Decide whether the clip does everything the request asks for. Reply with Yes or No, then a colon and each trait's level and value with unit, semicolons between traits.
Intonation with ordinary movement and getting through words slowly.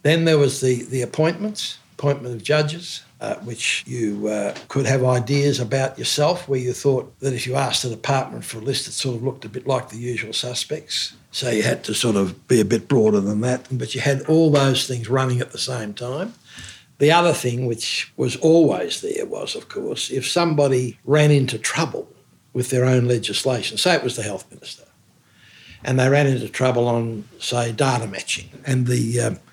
No: average, 3.0 semitones; fast, 205 wpm